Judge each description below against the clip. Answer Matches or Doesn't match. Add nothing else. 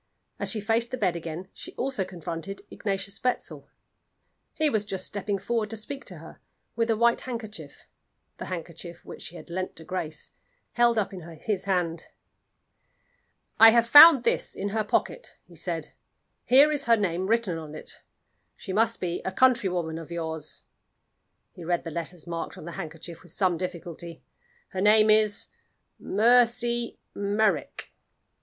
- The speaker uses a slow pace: Doesn't match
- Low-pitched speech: Doesn't match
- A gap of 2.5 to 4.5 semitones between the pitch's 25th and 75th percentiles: Doesn't match